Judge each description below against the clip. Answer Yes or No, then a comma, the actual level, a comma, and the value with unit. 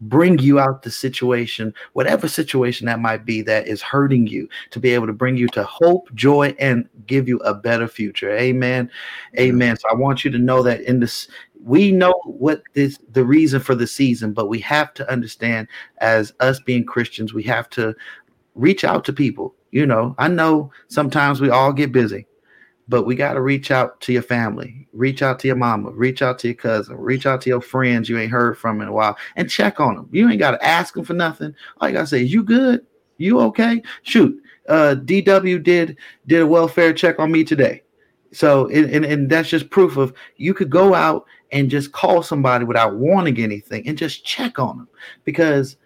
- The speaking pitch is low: Yes, low, 130 Hz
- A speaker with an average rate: No, fast, 215 wpm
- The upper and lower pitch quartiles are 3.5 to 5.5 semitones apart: Yes, average, 4.3 semitones